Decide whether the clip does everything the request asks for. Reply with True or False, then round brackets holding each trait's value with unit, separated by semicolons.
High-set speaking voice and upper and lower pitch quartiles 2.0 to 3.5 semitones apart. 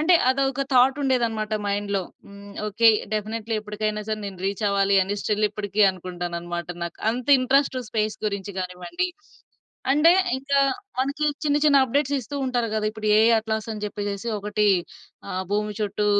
False (215 Hz; 4.1 semitones)